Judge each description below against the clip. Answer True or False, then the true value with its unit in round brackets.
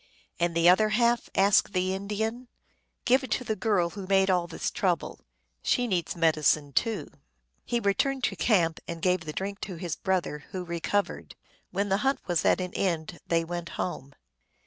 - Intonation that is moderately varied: True (3.7 semitones)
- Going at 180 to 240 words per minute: True (190 wpm)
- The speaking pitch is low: False (185 Hz)